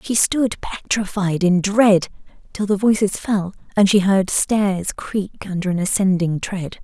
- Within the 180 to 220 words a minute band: No, average, 160 wpm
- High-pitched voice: Yes, high, 195 Hz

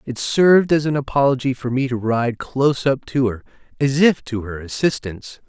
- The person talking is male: Yes, male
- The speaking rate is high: No, average, 195 wpm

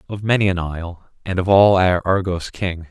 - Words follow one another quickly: No, average, 185 wpm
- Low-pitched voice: Yes, very low, 90 Hz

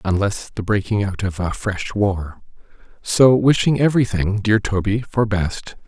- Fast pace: No, average, 155 wpm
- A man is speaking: Yes, male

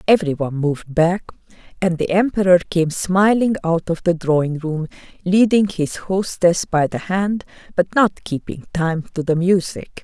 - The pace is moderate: Yes, average, 155 wpm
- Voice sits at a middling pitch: Yes, medium, 175 Hz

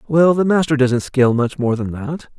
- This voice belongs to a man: Yes, male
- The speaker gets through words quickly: Yes, fast, 225 wpm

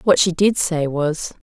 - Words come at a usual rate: No, fast, 210 wpm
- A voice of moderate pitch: Yes, medium, 170 Hz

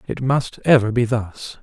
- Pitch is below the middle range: Yes, low, 120 Hz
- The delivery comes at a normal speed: Yes, average, 185 wpm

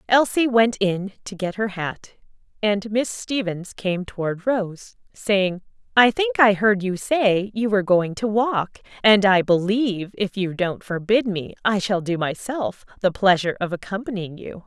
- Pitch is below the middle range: No, high, 200 Hz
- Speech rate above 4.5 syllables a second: No, 4.3 syllables/s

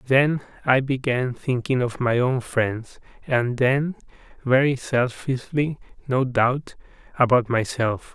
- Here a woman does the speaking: No, male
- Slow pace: Yes, slow, 120 wpm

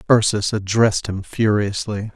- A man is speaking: Yes, male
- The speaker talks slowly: Yes, slow, 110 wpm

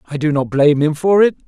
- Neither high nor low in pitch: Yes, medium, 155 Hz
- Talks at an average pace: No, fast, 285 wpm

